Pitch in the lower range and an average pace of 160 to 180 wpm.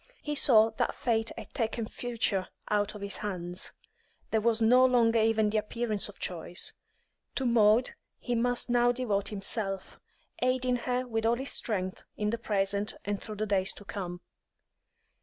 No: high, 220 Hz; average, 170 wpm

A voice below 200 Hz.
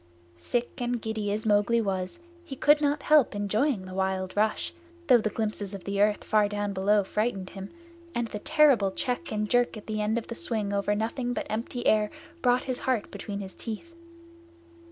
No: high, 215 Hz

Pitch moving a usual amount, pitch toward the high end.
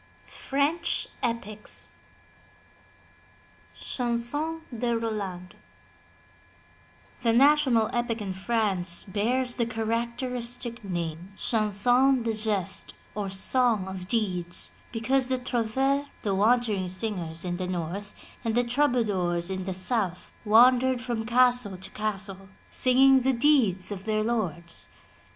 Yes: average, 4.4 semitones; high, 225 Hz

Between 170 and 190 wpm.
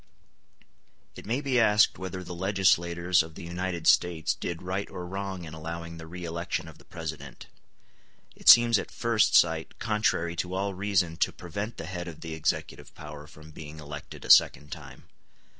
Yes: average, 175 wpm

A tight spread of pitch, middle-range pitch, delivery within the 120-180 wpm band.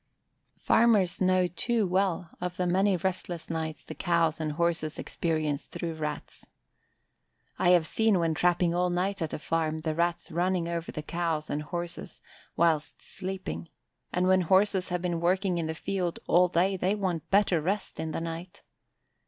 Yes: narrow, 2.2 semitones; medium, 175 Hz; average, 170 wpm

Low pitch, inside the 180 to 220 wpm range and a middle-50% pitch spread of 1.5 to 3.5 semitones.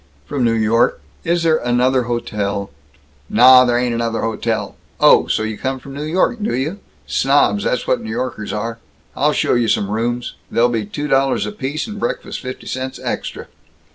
Yes: low, 120 Hz; average, 185 wpm; average, 3.2 semitones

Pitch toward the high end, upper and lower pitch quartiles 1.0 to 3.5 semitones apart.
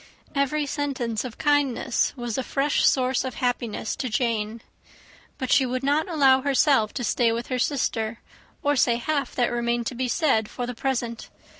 Yes: very high, 255 Hz; average, 2.8 semitones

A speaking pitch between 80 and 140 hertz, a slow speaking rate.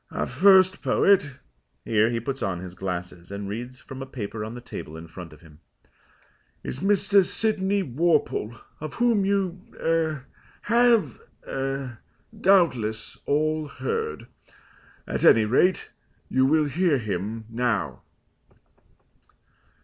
Yes: low, 135 Hz; slow, 125 wpm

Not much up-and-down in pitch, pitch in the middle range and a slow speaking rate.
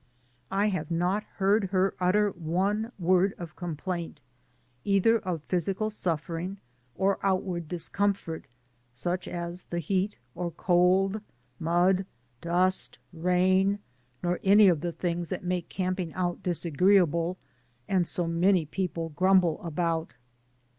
Yes: narrow, 2.2 semitones; medium, 180 Hz; slow, 120 wpm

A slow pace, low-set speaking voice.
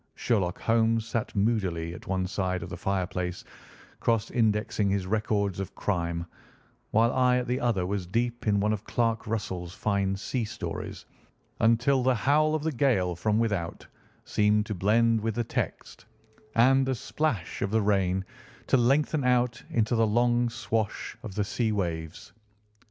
No: average, 160 wpm; low, 110 Hz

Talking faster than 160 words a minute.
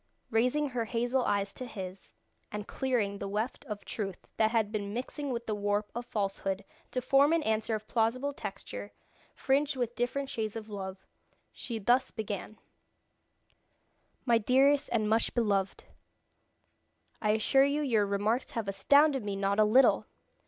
No: average, 155 wpm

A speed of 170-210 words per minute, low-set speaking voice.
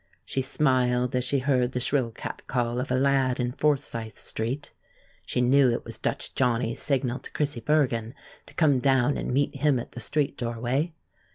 Yes: average, 180 wpm; low, 130 Hz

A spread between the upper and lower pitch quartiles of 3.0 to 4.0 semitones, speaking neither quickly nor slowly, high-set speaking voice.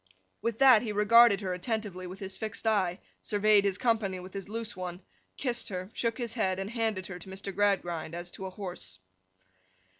Yes: average, 3.3 semitones; average, 190 wpm; high, 200 Hz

